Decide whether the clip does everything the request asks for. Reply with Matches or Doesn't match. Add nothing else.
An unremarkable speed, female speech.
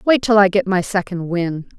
Doesn't match